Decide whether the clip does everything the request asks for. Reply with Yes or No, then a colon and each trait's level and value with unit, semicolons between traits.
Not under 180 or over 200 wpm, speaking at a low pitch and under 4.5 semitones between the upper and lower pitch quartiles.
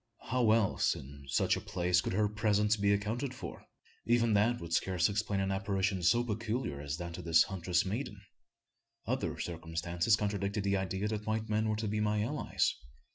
Yes: average, 185 wpm; low, 100 Hz; average, 3.5 semitones